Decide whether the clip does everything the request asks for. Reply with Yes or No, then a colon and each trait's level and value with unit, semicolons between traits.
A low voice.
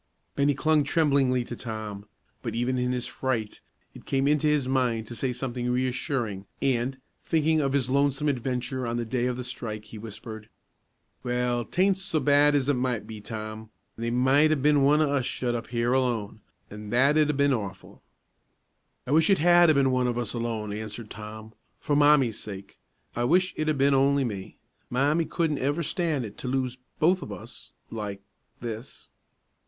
Yes: low, 125 Hz